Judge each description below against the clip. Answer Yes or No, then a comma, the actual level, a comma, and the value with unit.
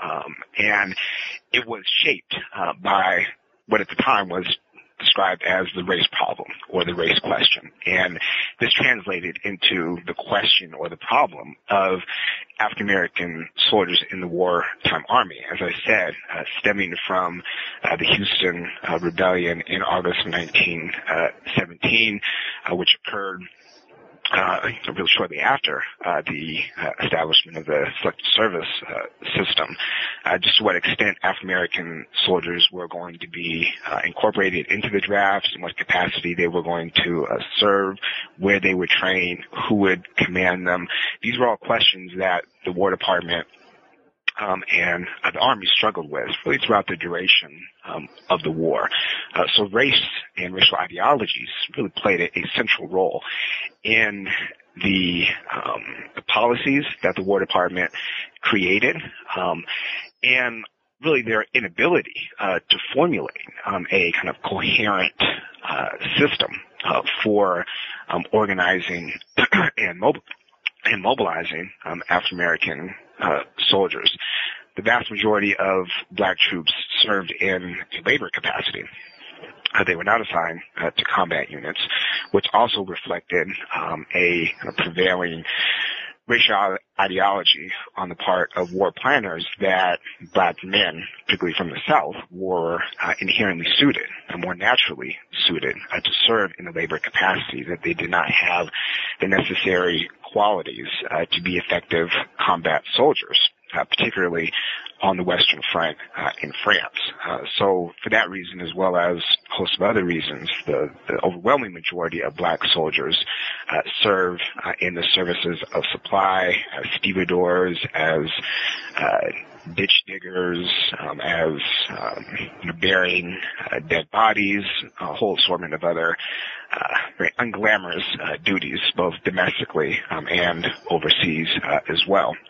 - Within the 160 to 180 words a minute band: No, average, 145 wpm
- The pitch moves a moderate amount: No, narrow, 2.0 semitones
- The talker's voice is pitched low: Yes, very low, 90 Hz